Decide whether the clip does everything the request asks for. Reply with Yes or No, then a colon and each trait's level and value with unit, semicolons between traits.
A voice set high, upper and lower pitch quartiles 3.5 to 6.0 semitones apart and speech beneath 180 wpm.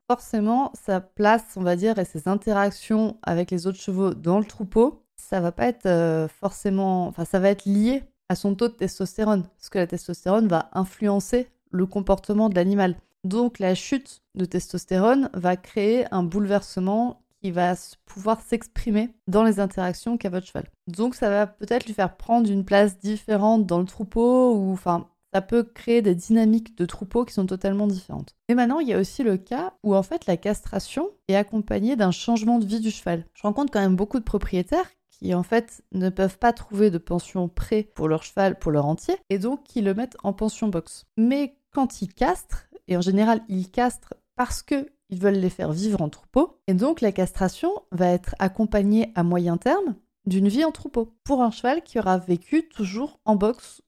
No: high, 205 Hz; average, 3.9 semitones; average, 200 wpm